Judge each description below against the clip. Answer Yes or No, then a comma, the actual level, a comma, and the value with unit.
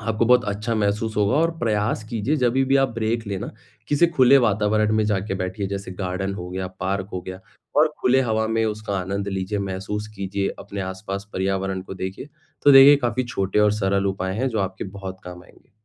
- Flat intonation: No, average, 3.1 semitones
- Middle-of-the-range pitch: No, low, 105 Hz